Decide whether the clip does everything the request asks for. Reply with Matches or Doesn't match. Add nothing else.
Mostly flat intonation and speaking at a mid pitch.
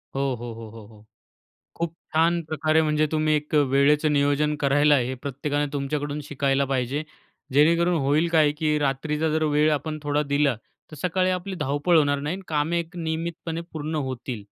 Matches